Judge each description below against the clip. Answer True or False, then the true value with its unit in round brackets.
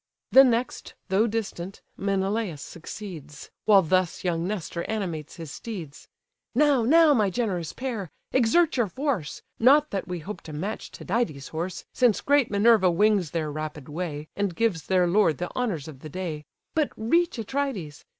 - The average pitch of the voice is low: False (195 Hz)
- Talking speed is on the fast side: False (160 wpm)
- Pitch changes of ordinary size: False (5.8 semitones)